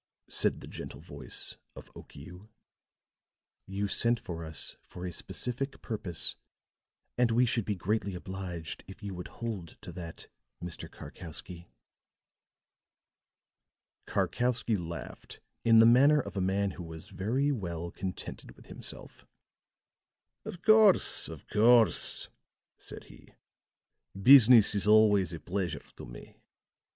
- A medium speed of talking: No, slow, 125 wpm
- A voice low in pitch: Yes, low, 100 Hz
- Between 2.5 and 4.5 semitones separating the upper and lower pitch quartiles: No, average, 5.0 semitones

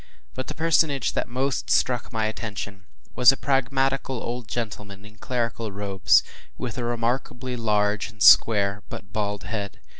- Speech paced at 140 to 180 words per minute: Yes, average, 155 wpm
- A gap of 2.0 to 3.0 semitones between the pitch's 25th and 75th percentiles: No, average, 3.7 semitones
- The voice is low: Yes, low, 115 Hz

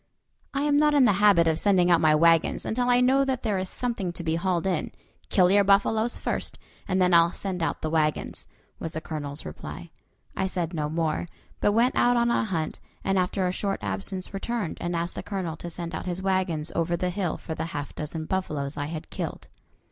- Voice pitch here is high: No, medium, 180 Hz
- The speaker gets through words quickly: Yes, fast, 220 wpm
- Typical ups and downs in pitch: Yes, average, 3.9 semitones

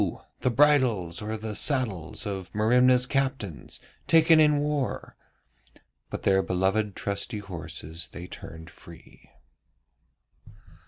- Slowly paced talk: Yes, slow, 105 wpm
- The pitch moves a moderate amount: No, wide, 6.2 semitones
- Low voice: Yes, low, 105 Hz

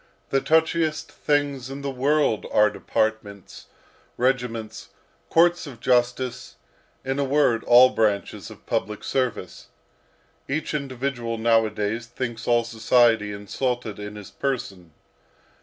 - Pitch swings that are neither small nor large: Yes, average, 3.7 semitones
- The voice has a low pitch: Yes, low, 120 Hz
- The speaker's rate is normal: No, slow, 115 wpm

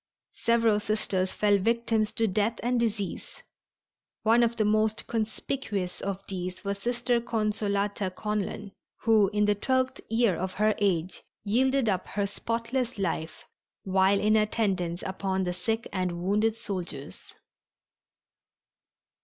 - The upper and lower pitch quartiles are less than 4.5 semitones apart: Yes, average, 2.9 semitones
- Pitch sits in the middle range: No, high, 210 Hz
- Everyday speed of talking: No, slow, 130 wpm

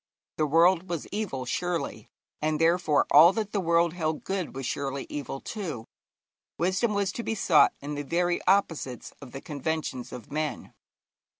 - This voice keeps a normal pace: Yes, average, 165 wpm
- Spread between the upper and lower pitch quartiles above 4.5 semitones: No, average, 4.1 semitones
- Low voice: No, medium, 165 Hz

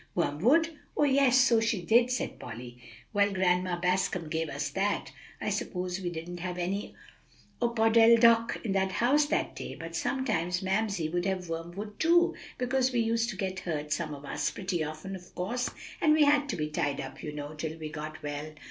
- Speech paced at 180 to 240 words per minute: Yes, average, 190 wpm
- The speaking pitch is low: No, high, 190 Hz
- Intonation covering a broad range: Yes, wide, 6.1 semitones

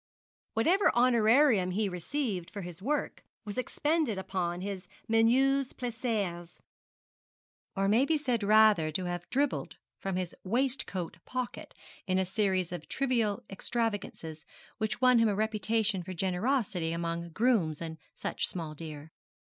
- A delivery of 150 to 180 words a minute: No, slow, 135 wpm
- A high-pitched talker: Yes, high, 205 Hz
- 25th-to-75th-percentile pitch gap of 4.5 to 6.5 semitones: Yes, wide, 5.4 semitones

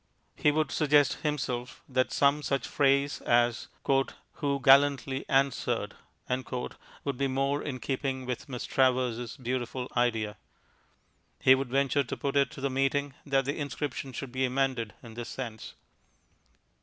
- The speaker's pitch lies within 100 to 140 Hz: Yes, low, 135 Hz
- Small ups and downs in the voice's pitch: Yes, narrow, 2.0 semitones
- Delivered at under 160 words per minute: Yes, average, 145 wpm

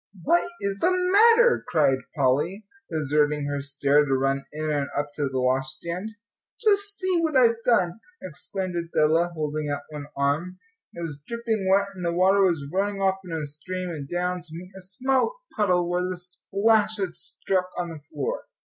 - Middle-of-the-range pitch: Yes, medium, 175 Hz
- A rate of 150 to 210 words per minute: Yes, average, 180 wpm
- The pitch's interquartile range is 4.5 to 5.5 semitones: Yes, average, 5.1 semitones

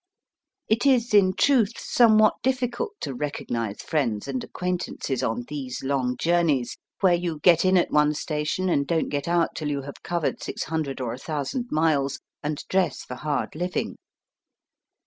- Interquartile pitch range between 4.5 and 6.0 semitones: Yes, average, 5.1 semitones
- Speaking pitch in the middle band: Yes, medium, 155 Hz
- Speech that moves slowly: No, average, 165 wpm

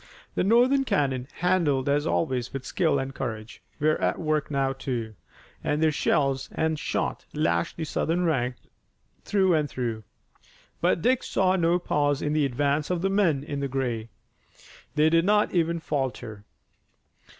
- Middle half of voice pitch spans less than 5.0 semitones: Yes, average, 4.1 semitones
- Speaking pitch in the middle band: Yes, medium, 150 Hz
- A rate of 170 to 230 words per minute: No, average, 155 wpm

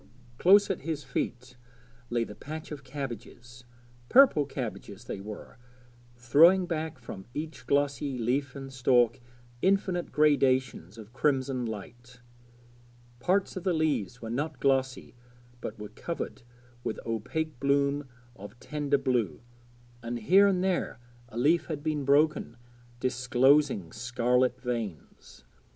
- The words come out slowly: Yes, slow, 125 wpm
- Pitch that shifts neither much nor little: Yes, average, 4.1 semitones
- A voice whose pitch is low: Yes, low, 130 Hz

